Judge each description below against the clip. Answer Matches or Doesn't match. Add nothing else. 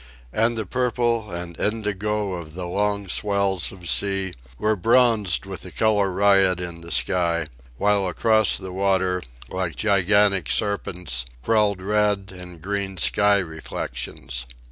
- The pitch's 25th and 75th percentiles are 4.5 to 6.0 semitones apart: Doesn't match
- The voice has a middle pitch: Doesn't match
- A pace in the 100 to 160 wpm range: Matches